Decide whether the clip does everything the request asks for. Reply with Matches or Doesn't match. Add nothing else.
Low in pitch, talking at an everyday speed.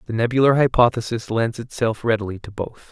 Matches